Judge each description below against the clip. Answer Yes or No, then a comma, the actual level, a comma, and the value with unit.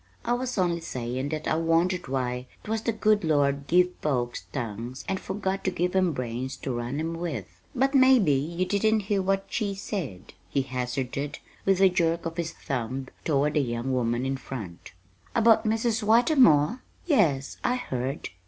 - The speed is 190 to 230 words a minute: No, average, 170 wpm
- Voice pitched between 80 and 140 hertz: No, medium, 160 Hz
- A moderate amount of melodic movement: No, wide, 7.0 semitones